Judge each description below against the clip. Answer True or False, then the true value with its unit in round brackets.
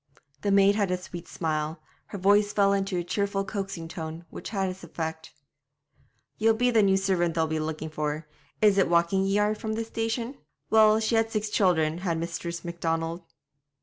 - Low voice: False (190 Hz)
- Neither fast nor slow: True (185 wpm)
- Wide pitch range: False (3.9 semitones)